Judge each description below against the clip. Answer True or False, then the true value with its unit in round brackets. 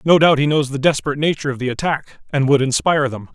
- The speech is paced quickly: True (250 wpm)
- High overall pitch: False (140 Hz)